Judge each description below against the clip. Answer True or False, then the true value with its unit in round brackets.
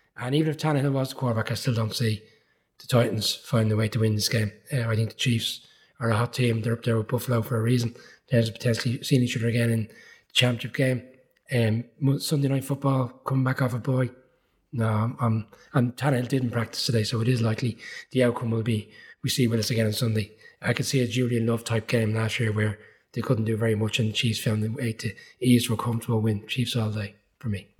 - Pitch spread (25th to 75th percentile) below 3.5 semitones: True (2.4 semitones)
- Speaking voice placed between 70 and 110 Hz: False (120 Hz)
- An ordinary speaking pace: False (245 wpm)